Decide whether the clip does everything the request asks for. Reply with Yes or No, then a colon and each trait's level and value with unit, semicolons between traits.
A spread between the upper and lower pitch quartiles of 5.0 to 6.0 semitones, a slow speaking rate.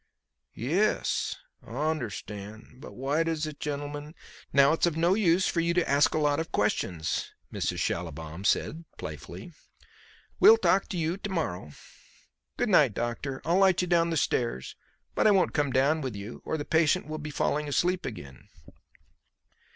No: average, 5.3 semitones; average, 170 wpm